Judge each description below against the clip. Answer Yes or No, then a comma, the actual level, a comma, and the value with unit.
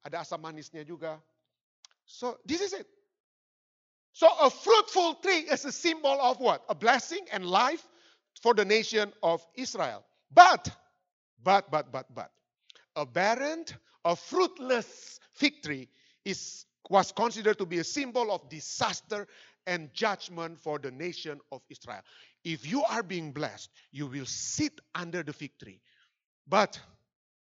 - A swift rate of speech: Yes, fast, 145 wpm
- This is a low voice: No, medium, 185 Hz